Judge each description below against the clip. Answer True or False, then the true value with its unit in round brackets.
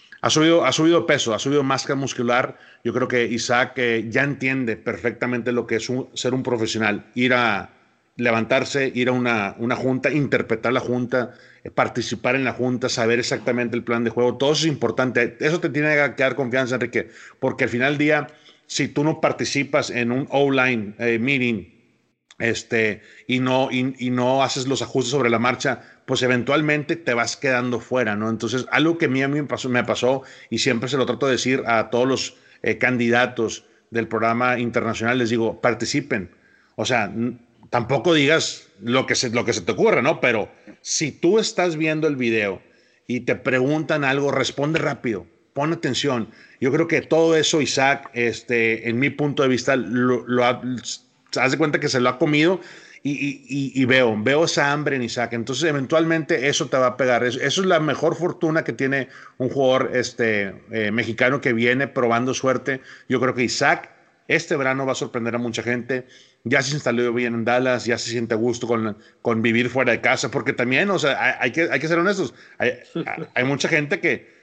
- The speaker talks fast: True (205 wpm)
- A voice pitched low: True (125 Hz)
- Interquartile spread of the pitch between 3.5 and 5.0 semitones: False (2.8 semitones)